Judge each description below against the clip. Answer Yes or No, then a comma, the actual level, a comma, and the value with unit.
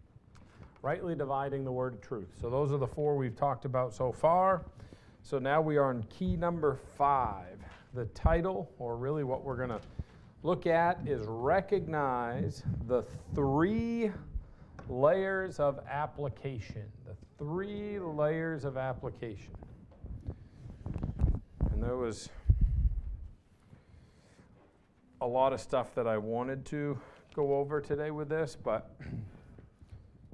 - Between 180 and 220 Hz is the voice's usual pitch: No, low, 135 Hz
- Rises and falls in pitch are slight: No, average, 5.0 semitones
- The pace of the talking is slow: Yes, slow, 125 wpm